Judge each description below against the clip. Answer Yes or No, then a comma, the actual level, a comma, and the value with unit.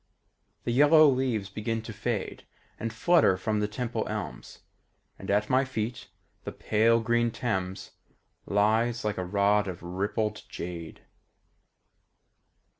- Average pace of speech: No, slow, 125 wpm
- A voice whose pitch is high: No, low, 110 Hz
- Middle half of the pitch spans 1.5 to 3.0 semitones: Yes, average, 2.7 semitones